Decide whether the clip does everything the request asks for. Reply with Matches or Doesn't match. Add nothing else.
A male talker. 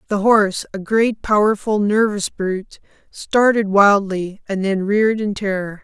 Doesn't match